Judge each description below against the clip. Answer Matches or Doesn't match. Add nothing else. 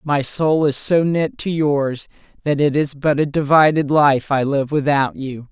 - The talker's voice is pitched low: Doesn't match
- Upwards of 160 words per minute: Matches